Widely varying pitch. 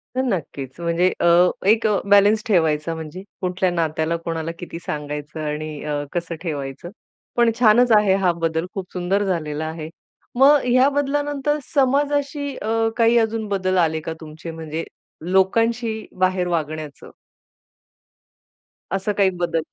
Yes: wide, 6.0 semitones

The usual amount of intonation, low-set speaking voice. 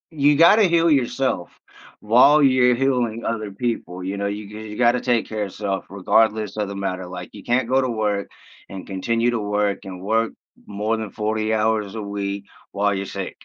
Yes: average, 3.2 semitones; low, 110 Hz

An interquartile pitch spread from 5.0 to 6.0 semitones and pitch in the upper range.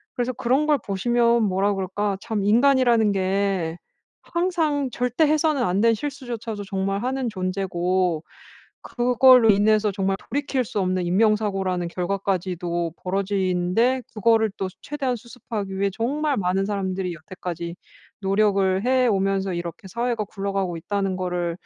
No: average, 4.3 semitones; high, 200 Hz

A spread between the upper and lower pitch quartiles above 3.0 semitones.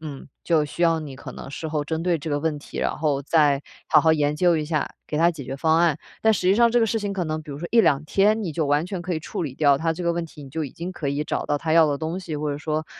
No: average, 2.7 semitones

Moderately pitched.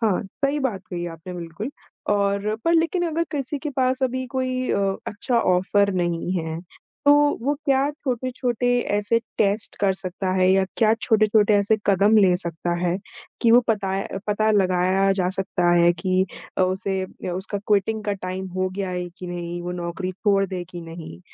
No: high, 195 Hz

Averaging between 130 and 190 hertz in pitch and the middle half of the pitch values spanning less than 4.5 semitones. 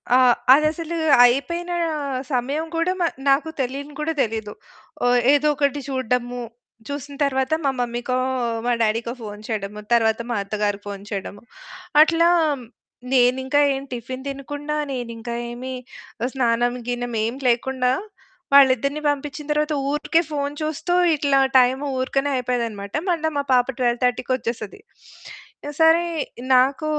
No: very high, 260 Hz; average, 3.4 semitones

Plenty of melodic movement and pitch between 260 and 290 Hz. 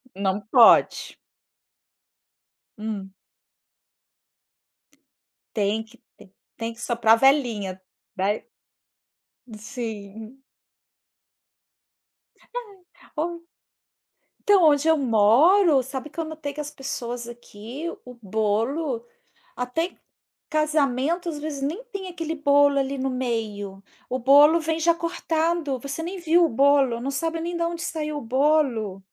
Yes: wide, 5.9 semitones; very high, 275 Hz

